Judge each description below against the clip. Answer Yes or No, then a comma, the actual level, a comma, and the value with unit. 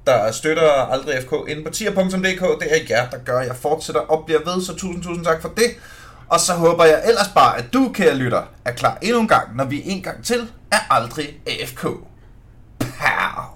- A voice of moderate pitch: Yes, medium, 165 Hz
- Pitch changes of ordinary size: Yes, average, 4.1 semitones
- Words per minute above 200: Yes, average, 215 wpm